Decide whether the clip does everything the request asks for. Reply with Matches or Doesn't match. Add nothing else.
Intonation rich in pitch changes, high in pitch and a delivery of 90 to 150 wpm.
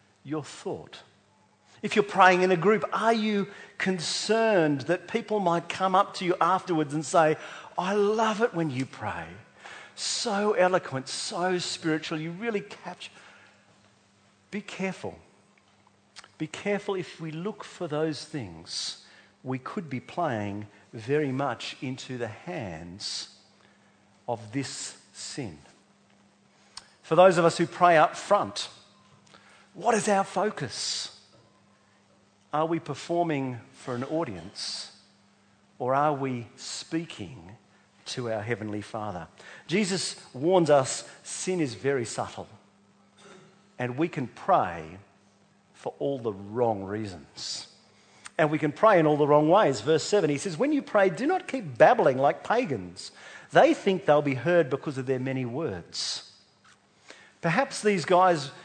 Doesn't match